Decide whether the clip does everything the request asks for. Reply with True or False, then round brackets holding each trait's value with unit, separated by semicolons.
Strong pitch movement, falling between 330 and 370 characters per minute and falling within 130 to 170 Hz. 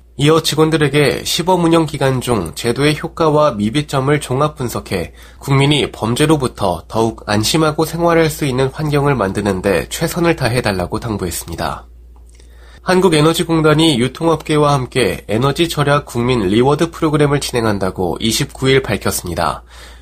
True (7.3 semitones; 335 characters per minute; 135 Hz)